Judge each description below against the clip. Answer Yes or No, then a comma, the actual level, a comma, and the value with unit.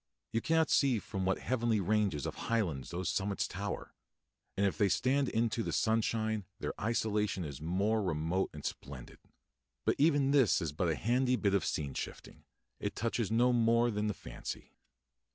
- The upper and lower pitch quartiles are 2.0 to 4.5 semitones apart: Yes, average, 3.9 semitones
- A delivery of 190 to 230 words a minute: No, average, 175 wpm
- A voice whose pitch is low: Yes, low, 105 Hz